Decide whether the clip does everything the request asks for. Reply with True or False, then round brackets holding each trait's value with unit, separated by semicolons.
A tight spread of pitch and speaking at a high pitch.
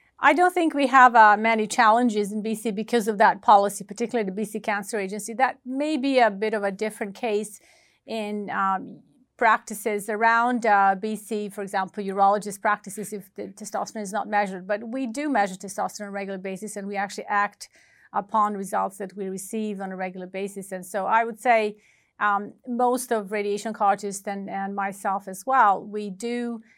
True (2.2 semitones; 210 Hz)